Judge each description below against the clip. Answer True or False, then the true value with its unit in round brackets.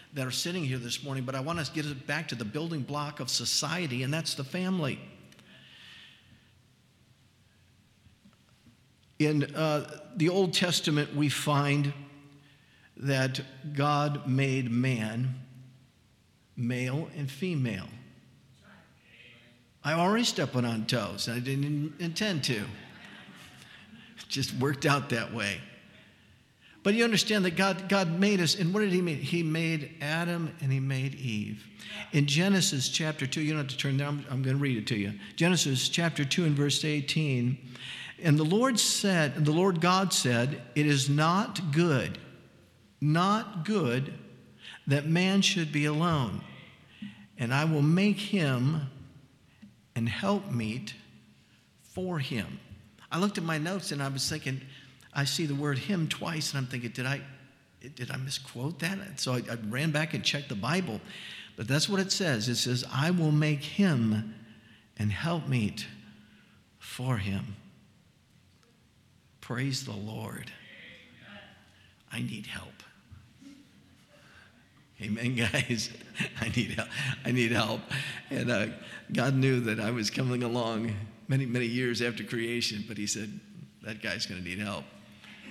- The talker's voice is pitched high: False (135 Hz)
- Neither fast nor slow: True (150 wpm)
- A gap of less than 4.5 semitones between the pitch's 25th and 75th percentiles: False (4.8 semitones)